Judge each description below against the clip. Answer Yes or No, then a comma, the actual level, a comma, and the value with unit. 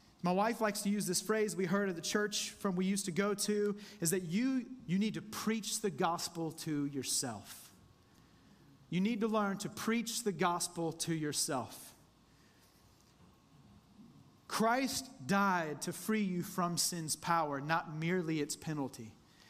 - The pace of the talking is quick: No, average, 155 wpm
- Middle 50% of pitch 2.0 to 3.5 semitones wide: No, average, 4.7 semitones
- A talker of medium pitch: Yes, medium, 180 Hz